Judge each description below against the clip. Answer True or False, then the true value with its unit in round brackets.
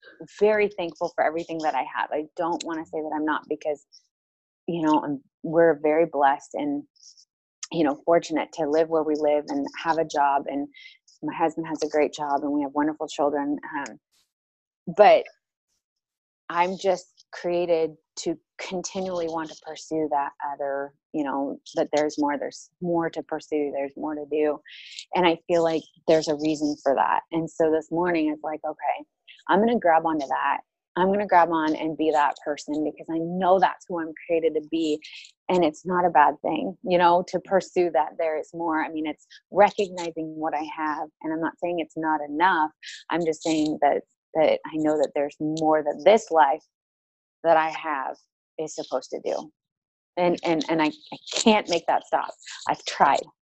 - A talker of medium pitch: True (160 Hz)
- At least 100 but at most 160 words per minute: False (190 wpm)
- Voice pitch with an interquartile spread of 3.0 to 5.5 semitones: False (2.4 semitones)